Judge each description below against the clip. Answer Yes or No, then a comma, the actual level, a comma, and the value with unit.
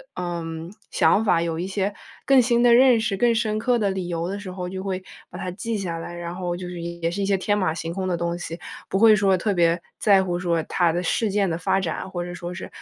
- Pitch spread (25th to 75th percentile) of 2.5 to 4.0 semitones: Yes, average, 2.9 semitones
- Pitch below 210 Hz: Yes, medium, 185 Hz